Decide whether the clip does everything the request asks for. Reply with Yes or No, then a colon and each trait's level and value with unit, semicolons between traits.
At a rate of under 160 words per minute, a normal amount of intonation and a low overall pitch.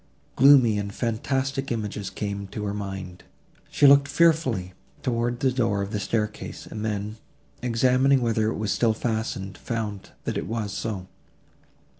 Yes: average, 150 wpm; average, 3.5 semitones; low, 110 Hz